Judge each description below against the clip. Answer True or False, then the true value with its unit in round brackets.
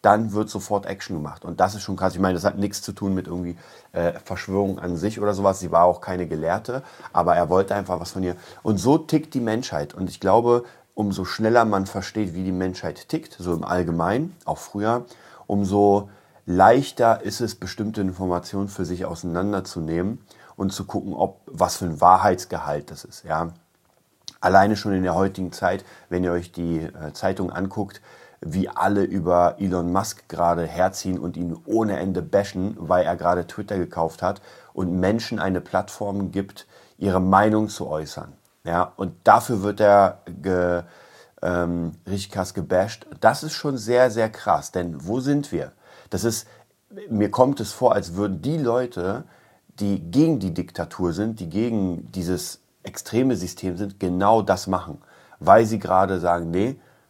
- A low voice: True (95 Hz)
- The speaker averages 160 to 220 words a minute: True (175 wpm)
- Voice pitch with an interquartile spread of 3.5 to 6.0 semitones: False (2.9 semitones)